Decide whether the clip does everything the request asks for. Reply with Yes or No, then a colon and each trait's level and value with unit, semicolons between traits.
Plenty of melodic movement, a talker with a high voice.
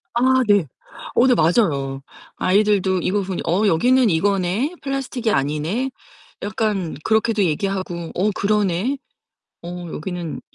No: average, 4.6 semitones; high, 200 Hz